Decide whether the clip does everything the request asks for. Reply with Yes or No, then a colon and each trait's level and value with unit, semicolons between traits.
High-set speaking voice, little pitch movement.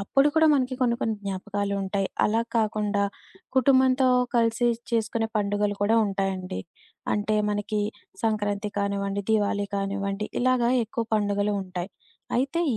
Yes: high, 210 Hz; narrow, 2.3 semitones